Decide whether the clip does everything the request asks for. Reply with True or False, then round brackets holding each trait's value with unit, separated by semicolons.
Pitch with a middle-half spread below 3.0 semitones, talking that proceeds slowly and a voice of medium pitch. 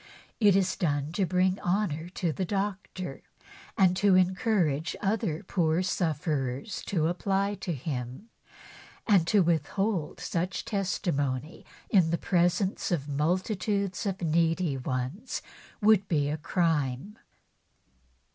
False (4.1 semitones; 120 wpm; 175 Hz)